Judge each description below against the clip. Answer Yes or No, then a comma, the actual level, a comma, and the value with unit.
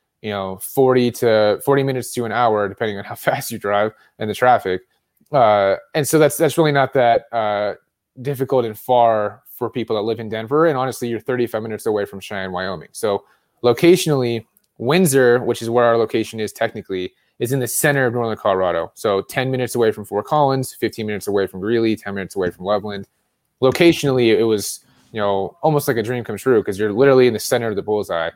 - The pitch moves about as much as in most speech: Yes, average, 3.9 semitones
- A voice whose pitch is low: Yes, low, 115 Hz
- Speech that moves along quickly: Yes, fast, 210 wpm